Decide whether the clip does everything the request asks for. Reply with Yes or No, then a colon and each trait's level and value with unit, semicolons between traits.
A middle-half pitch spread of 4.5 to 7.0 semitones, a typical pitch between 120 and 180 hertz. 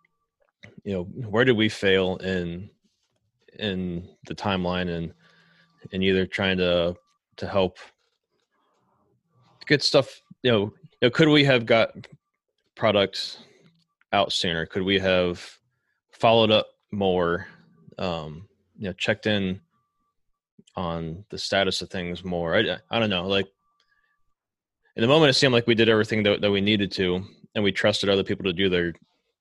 No: average, 4.8 semitones; low, 100 Hz